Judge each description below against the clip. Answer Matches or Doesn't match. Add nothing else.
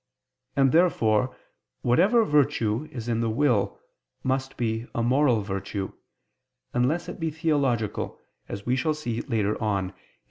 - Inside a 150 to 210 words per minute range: Doesn't match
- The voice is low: Matches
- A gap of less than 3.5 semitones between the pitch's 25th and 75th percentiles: Doesn't match